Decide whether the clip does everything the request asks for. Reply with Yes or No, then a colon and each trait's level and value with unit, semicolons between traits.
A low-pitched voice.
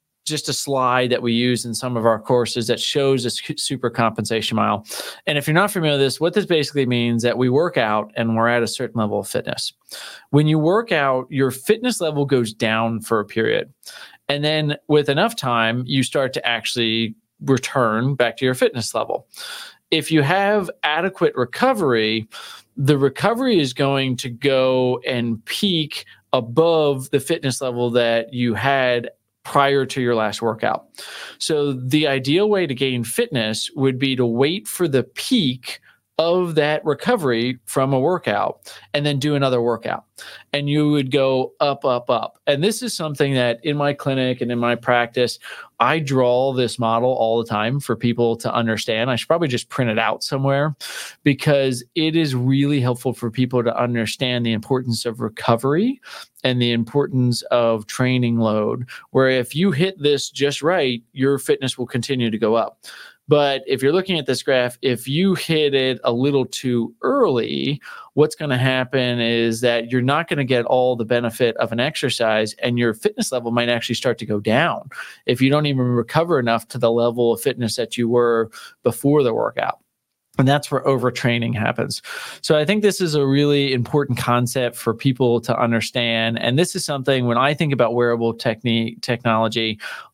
Yes: low, 130 Hz